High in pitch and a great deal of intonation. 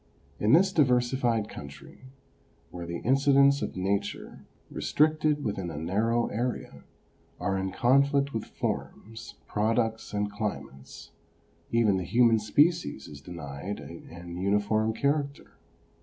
No: low, 110 Hz; wide, 6.1 semitones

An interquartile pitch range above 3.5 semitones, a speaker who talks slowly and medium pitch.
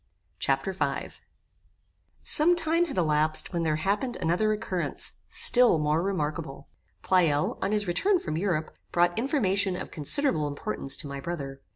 No: wide, 5.5 semitones; average, 145 wpm; medium, 175 Hz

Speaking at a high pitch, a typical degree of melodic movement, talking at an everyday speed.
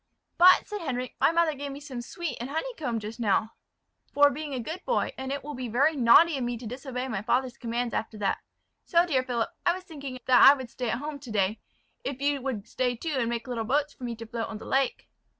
No: very high, 255 Hz; average, 3.6 semitones; fast, 245 wpm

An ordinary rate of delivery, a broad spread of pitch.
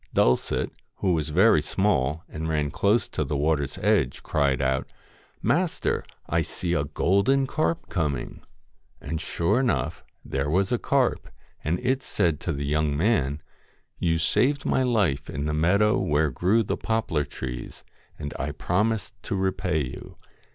Yes: average, 160 wpm; wide, 6.2 semitones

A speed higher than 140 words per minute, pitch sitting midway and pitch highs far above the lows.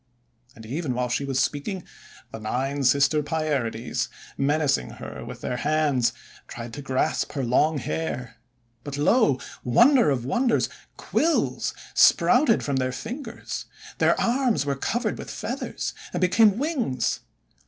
No: slow, 135 wpm; medium, 145 Hz; wide, 7.4 semitones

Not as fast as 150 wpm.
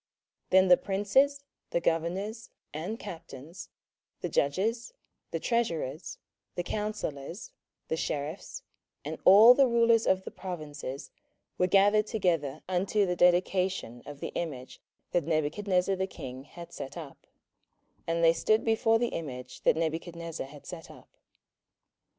Yes: slow, 135 wpm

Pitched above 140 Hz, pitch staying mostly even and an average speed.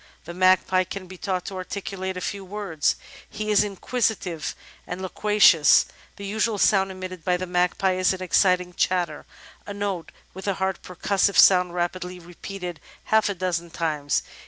Yes: medium, 185 Hz; narrow, 1.8 semitones; average, 165 wpm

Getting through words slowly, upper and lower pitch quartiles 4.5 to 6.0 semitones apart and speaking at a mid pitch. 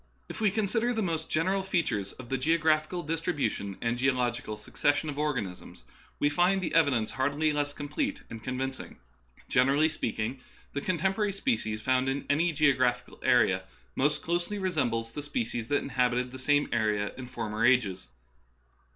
No: average, 160 wpm; average, 5.1 semitones; medium, 145 Hz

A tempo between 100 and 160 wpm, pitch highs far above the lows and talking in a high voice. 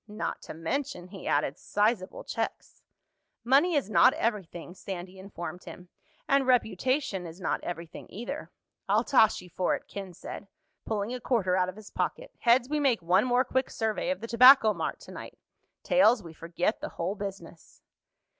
No: average, 170 wpm; wide, 5.8 semitones; high, 210 Hz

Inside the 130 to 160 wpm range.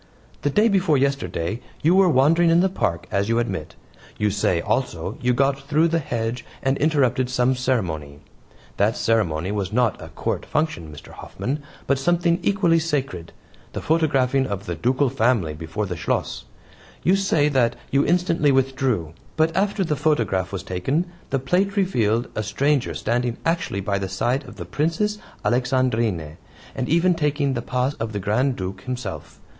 No: average, 170 wpm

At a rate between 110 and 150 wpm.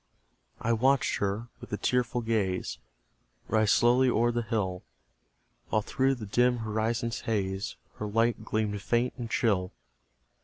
Yes: average, 140 wpm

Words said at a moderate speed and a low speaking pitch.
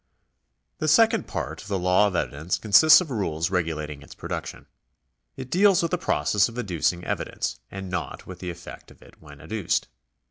Yes: average, 180 wpm; very low, 95 Hz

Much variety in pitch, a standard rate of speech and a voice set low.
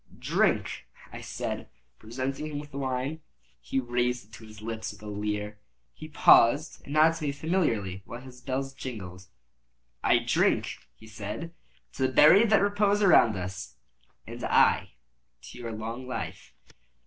Yes: wide, 5.7 semitones; average, 155 wpm; low, 125 Hz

